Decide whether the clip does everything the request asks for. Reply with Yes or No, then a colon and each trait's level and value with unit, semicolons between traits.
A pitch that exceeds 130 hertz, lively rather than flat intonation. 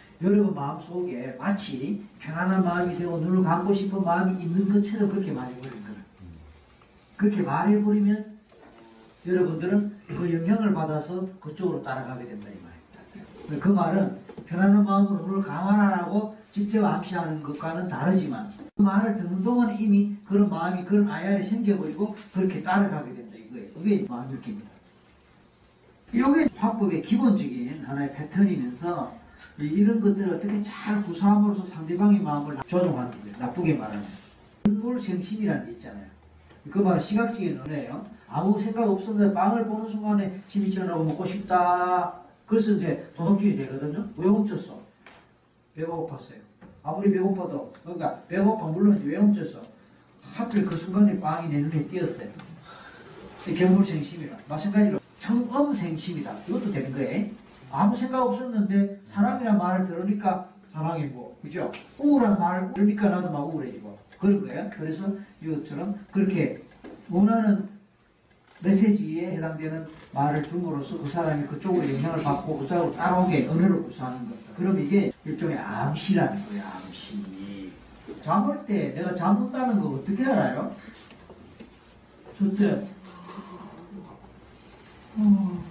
No: high, 190 Hz; average, 4.0 semitones